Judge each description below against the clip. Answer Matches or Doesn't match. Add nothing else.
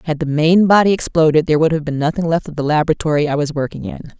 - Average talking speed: Doesn't match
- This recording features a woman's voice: Matches